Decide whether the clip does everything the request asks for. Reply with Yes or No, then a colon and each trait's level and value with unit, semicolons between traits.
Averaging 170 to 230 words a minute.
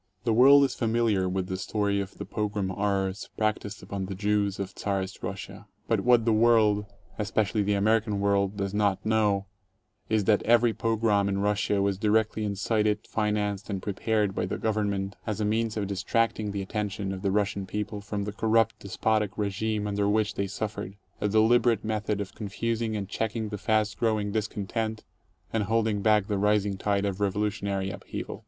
Yes: average, 190 wpm